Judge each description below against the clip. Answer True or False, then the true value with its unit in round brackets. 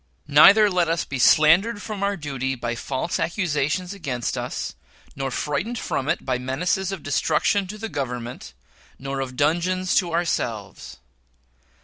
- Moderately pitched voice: True (155 Hz)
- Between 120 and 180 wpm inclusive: True (145 wpm)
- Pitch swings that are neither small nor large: False (5.8 semitones)